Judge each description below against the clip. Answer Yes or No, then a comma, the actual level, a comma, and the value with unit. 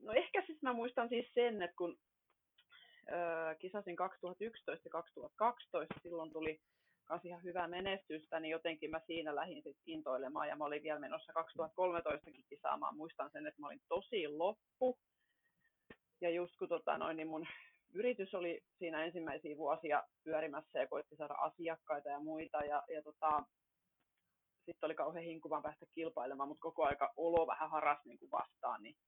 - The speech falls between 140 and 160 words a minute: Yes, fast, 155 wpm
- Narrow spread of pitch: No, average, 3.7 semitones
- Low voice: No, medium, 165 Hz